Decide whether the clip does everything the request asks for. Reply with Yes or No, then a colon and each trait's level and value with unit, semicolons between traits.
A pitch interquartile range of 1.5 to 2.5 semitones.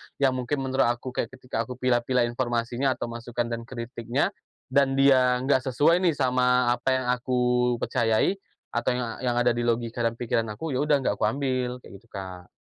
Yes: narrow, 1.9 semitones